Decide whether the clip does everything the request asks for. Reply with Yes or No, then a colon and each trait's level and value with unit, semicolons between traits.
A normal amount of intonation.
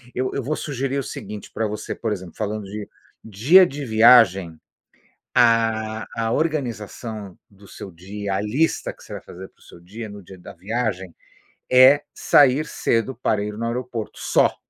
Yes: average, 3.9 semitones